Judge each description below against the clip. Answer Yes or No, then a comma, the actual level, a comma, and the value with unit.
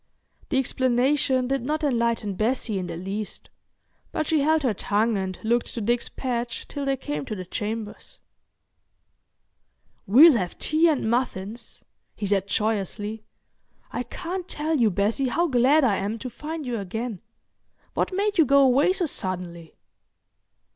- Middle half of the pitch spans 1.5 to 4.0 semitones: No, average, 5.3 semitones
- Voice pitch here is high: Yes, high, 240 Hz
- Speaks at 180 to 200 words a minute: No, average, 155 wpm